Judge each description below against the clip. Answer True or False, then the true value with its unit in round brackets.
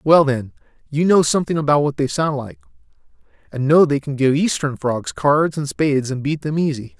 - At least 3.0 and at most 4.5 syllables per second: False (5.4 syllables/s)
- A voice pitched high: False (145 Hz)